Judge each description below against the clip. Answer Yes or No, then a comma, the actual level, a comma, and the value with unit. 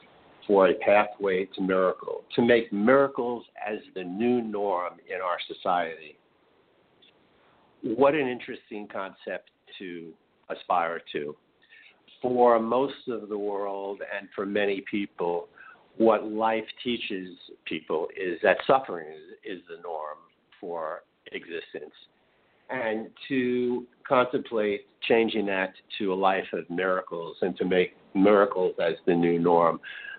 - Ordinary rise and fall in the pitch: No, wide, 6.0 semitones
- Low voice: Yes, low, 110 Hz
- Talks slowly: Yes, slow, 125 wpm